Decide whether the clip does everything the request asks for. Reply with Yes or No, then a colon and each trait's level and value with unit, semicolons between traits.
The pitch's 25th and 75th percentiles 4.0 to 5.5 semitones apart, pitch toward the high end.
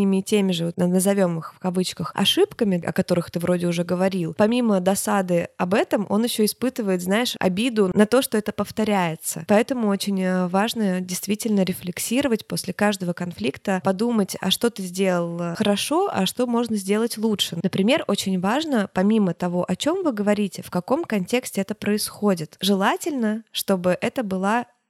No: average, 3.3 semitones; high, 200 Hz